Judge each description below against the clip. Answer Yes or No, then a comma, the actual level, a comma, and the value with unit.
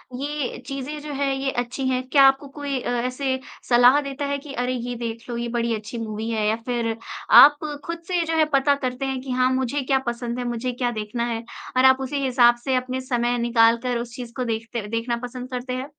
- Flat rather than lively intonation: Yes, narrow, 2.3 semitones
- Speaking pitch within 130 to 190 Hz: No, very high, 250 Hz